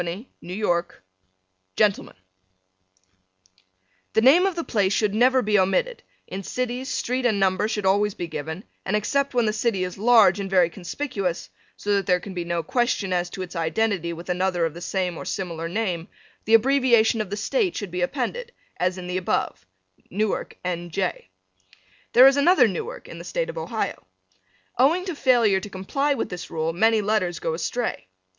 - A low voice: No, high, 200 Hz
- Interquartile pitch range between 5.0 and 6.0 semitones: Yes, wide, 5.4 semitones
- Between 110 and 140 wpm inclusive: No, average, 180 wpm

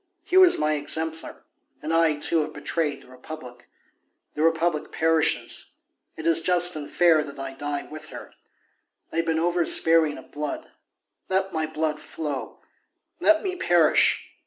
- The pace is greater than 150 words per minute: Yes, average, 160 wpm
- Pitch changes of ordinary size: No, narrow, 1.7 semitones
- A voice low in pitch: No, medium, 160 Hz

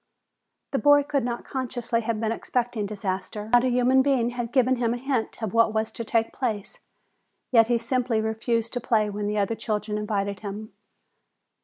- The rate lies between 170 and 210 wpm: Yes, average, 185 wpm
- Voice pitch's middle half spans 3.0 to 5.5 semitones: No, narrow, 2.4 semitones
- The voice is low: No, high, 230 Hz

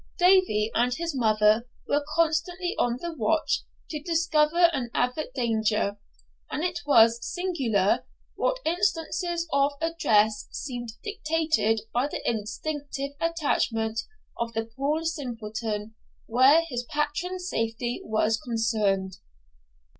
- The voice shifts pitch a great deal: Yes, wide, 6.5 semitones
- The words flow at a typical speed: No, slow, 115 wpm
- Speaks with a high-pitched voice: Yes, very high, 265 Hz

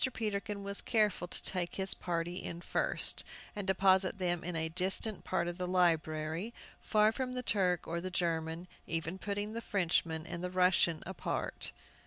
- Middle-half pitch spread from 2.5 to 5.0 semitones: Yes, average, 2.8 semitones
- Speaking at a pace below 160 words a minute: No, average, 165 wpm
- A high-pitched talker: No, medium, 180 Hz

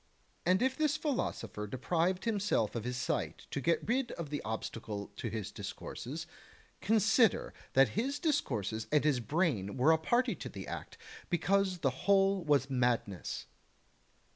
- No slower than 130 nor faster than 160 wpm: Yes, average, 150 wpm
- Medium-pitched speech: Yes, medium, 155 Hz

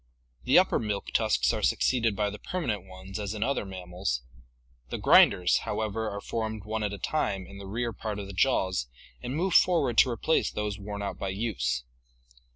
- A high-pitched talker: No, low, 105 Hz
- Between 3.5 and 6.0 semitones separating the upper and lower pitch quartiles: No, average, 3.0 semitones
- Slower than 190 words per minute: No, average, 195 wpm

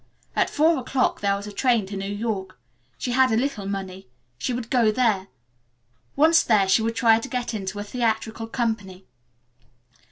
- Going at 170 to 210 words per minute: Yes, average, 185 wpm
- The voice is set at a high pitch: Yes, high, 225 Hz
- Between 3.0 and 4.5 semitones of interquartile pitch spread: Yes, average, 3.9 semitones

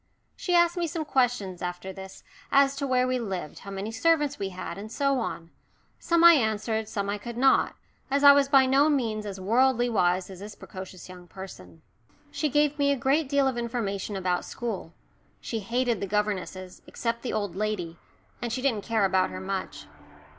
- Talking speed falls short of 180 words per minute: No, average, 195 wpm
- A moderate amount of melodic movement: No, wide, 6.0 semitones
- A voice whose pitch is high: Yes, high, 225 Hz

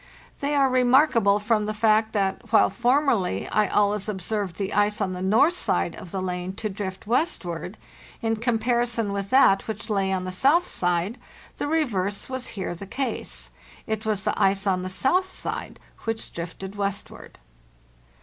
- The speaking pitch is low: No, high, 210 Hz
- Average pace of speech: Yes, average, 170 wpm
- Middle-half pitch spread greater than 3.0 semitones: Yes, average, 3.9 semitones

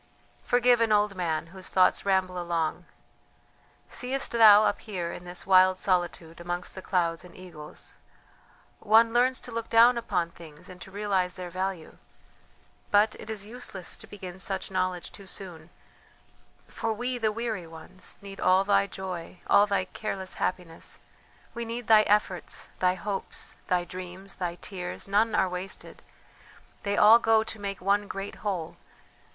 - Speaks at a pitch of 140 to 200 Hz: Yes, high, 190 Hz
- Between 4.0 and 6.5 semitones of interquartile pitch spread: No, average, 2.9 semitones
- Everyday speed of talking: Yes, average, 155 wpm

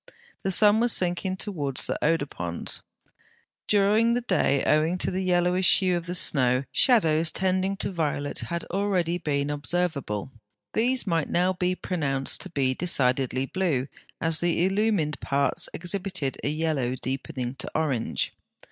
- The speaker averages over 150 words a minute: No, average, 145 wpm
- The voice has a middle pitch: Yes, medium, 170 Hz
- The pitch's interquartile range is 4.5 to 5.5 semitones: Yes, average, 4.9 semitones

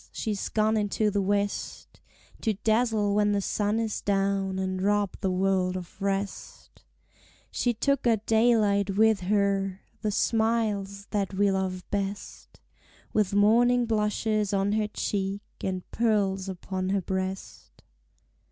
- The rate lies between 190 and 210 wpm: No, slow, 135 wpm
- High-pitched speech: Yes, high, 205 Hz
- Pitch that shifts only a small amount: Yes, narrow, 1.9 semitones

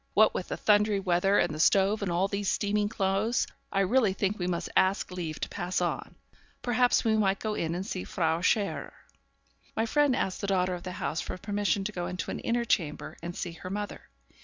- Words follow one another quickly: Yes, fast, 215 wpm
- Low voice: No, high, 195 Hz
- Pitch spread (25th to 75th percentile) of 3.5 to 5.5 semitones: No, average, 2.7 semitones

